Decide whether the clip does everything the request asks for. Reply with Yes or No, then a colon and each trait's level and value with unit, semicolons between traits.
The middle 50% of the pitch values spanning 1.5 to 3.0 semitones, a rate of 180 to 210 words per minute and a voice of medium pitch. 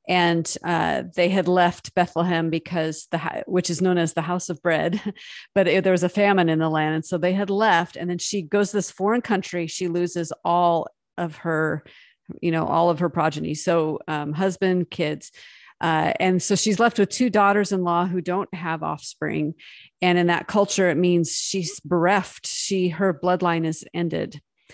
Yes: narrow, 2.4 semitones; average, 195 wpm; medium, 175 Hz